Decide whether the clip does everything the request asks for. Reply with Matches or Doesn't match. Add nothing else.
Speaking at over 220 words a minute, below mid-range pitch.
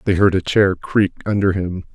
Doesn't match